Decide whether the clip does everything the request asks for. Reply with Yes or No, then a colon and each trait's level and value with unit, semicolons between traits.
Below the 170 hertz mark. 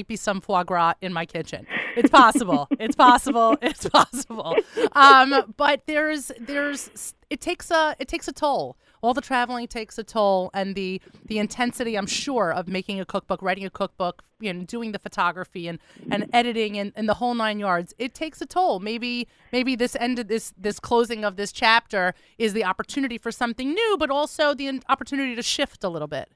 No: high, 235 Hz